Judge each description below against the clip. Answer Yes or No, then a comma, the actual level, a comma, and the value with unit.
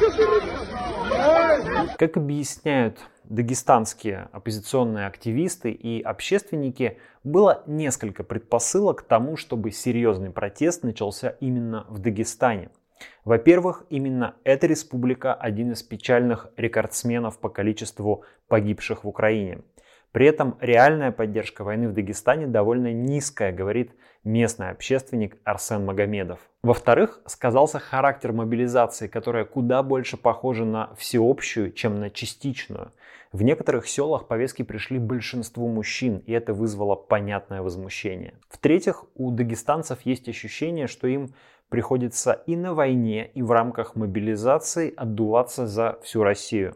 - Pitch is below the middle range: Yes, low, 115 Hz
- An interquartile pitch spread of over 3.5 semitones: No, average, 2.9 semitones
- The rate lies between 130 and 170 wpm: No, average, 115 wpm